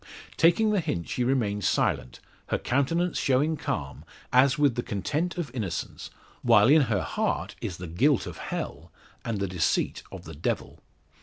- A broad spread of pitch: Yes, wide, 7.3 semitones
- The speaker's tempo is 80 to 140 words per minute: No, average, 165 wpm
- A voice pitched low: Yes, low, 125 Hz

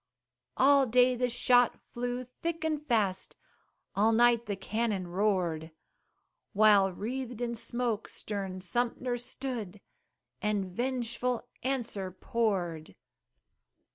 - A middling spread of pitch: Yes, average, 3.8 semitones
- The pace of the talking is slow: Yes, slow, 105 wpm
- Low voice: No, high, 230 Hz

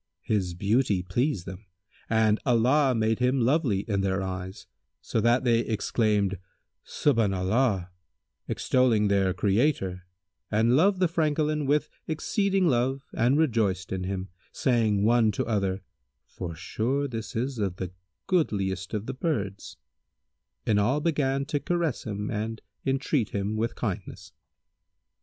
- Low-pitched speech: Yes, low, 110 Hz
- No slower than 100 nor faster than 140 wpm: Yes, slow, 135 wpm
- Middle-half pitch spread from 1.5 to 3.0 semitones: No, wide, 5.4 semitones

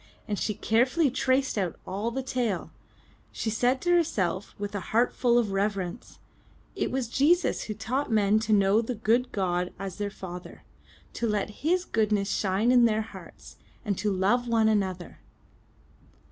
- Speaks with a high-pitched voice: Yes, high, 220 Hz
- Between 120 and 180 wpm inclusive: Yes, average, 165 wpm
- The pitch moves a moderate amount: Yes, average, 3.6 semitones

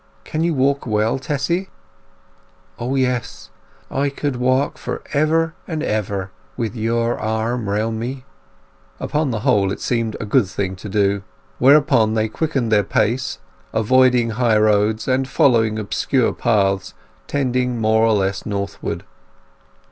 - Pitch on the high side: No, low, 115 Hz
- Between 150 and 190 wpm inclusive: No, average, 140 wpm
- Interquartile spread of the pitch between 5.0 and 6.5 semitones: No, average, 3.7 semitones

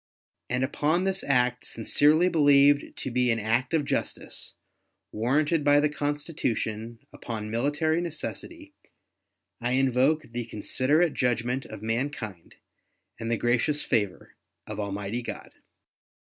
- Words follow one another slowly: Yes, slow, 120 wpm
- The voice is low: Yes, low, 130 Hz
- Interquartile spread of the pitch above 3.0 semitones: Yes, average, 4.3 semitones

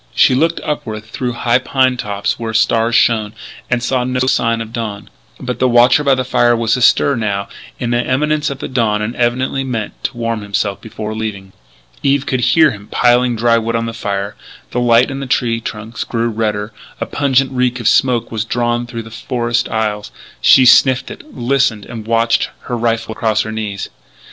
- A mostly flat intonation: Yes, narrow, 2.3 semitones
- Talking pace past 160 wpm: Yes, average, 195 wpm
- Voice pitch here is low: Yes, low, 120 Hz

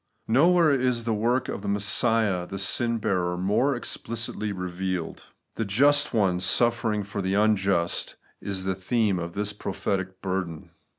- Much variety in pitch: No, average, 3.8 semitones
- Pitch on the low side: Yes, low, 100 Hz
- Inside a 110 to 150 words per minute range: Yes, average, 140 wpm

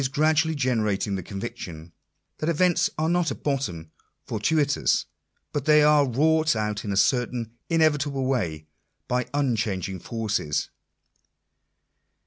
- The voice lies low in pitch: Yes, low, 125 Hz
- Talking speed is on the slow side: Yes, slow, 125 wpm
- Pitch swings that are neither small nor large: No, wide, 6.5 semitones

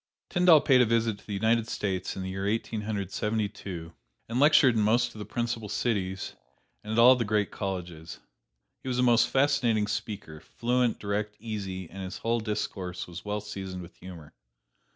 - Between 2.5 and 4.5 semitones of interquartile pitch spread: Yes, average, 3.6 semitones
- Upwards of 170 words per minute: Yes, average, 190 wpm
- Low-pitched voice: Yes, low, 105 Hz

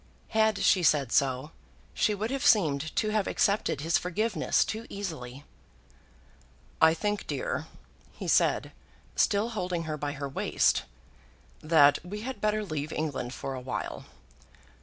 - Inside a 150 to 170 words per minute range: No, average, 140 wpm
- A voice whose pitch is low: No, medium, 170 Hz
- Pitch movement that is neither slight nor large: No, wide, 6.7 semitones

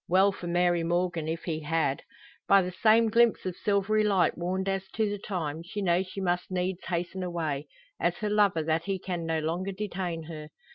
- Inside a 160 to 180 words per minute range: No, average, 200 wpm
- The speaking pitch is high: No, medium, 180 Hz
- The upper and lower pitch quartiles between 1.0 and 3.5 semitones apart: Yes, average, 2.8 semitones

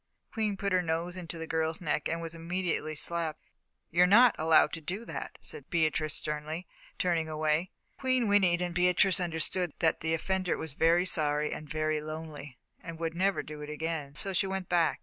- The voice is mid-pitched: Yes, medium, 165 Hz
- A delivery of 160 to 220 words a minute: Yes, average, 190 wpm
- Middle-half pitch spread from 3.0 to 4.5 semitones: No, narrow, 2.6 semitones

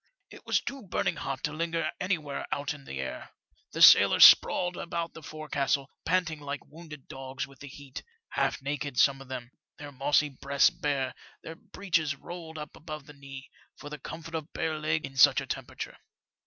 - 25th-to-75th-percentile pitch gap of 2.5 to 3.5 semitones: Yes, average, 2.8 semitones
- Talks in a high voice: No, medium, 150 Hz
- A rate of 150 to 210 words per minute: Yes, average, 190 wpm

